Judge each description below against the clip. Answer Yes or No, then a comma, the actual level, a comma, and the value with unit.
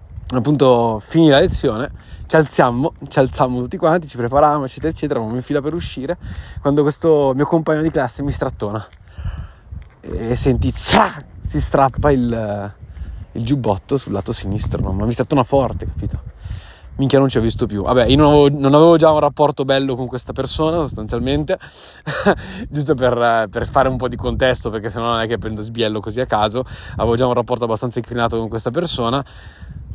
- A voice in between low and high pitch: No, low, 125 Hz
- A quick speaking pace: Yes, fast, 185 wpm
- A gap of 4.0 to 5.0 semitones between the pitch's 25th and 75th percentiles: Yes, average, 4.4 semitones